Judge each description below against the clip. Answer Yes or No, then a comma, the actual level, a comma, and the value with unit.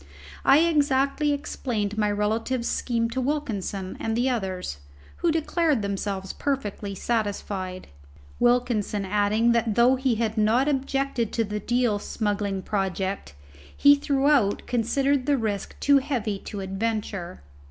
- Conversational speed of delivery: No, slow, 130 wpm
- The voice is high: Yes, high, 225 Hz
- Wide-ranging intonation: No, average, 4.7 semitones